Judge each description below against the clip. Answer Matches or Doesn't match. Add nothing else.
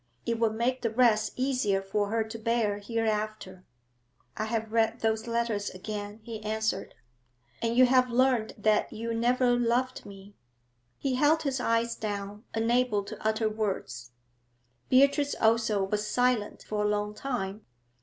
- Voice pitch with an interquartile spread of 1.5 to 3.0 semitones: Matches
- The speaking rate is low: Doesn't match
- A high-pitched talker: Matches